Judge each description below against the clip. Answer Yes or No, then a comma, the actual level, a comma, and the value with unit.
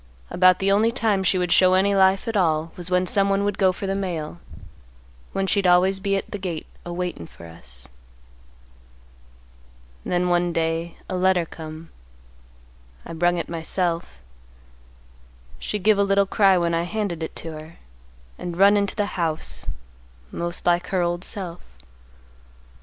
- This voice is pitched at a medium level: Yes, medium, 180 Hz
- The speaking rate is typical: Yes, average, 160 wpm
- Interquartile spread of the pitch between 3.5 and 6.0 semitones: No, average, 2.7 semitones